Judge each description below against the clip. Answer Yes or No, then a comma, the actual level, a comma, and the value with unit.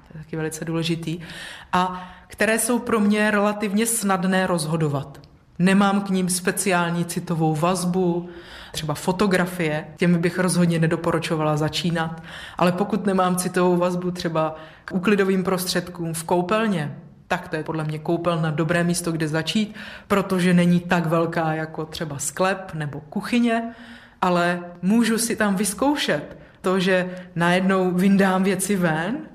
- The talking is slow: No, average, 135 wpm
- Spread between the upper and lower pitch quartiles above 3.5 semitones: No, average, 2.8 semitones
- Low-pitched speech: No, medium, 180 Hz